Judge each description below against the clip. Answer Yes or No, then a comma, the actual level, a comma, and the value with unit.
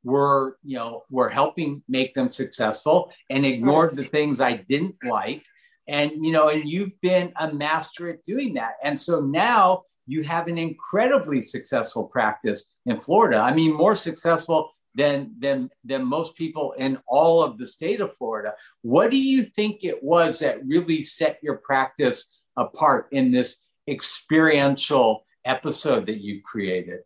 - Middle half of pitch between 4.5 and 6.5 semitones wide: Yes, average, 5.1 semitones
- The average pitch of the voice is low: No, medium, 160 Hz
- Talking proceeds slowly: No, average, 160 wpm